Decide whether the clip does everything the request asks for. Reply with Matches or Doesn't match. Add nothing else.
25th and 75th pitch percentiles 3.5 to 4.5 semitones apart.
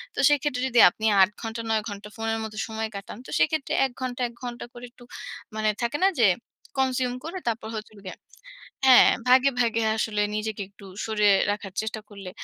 Doesn't match